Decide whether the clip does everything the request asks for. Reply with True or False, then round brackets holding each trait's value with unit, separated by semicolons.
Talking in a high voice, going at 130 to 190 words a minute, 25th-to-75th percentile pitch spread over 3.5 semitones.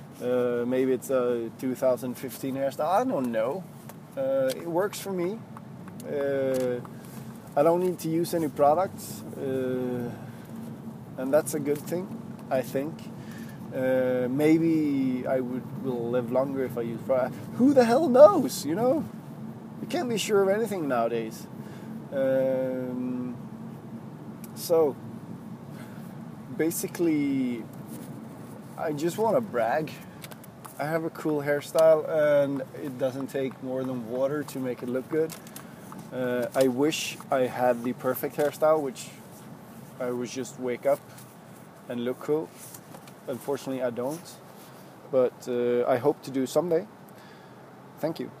False (135 Hz; 140 wpm; 4.4 semitones)